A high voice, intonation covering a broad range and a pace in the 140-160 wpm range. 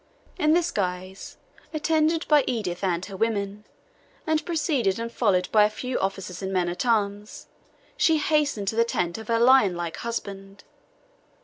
Yes: high, 215 Hz; wide, 5.7 semitones; average, 155 wpm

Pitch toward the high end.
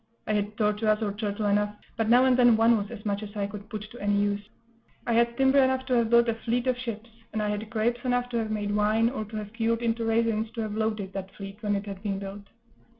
Yes: high, 220 Hz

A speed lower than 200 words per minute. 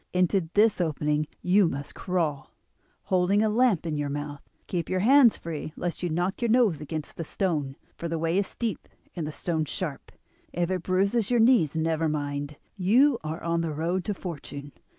Yes: average, 190 wpm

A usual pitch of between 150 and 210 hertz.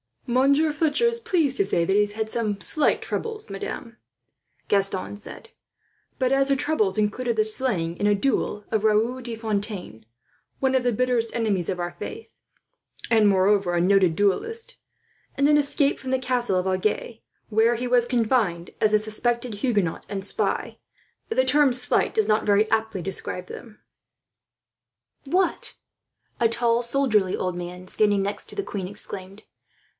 No: high, 220 Hz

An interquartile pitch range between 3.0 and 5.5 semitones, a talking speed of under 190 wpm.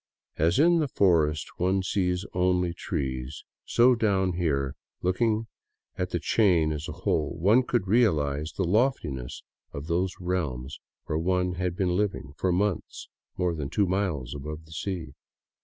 Yes: average, 4.0 semitones; average, 155 wpm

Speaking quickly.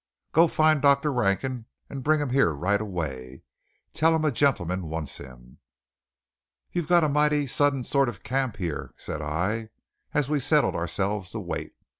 No: average, 165 wpm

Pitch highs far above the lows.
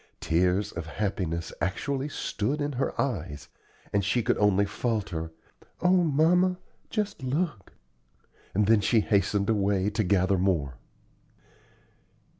Yes: wide, 6.4 semitones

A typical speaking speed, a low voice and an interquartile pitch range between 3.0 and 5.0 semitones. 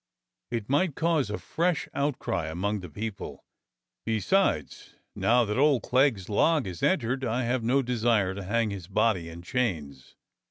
No: average, 155 wpm; low, 115 Hz; wide, 5.4 semitones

